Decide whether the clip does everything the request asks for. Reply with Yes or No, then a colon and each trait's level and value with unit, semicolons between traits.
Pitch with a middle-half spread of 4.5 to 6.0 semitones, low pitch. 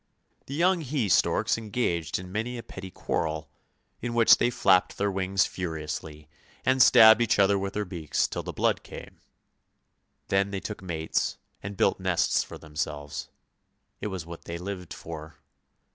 Yes: average, 5.3 semitones; very low, 95 Hz